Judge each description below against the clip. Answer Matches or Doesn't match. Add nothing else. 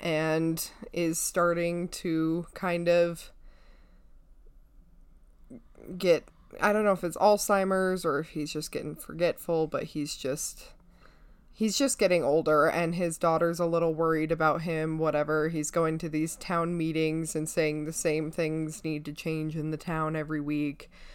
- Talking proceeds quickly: Doesn't match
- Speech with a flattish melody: Matches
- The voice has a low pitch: Doesn't match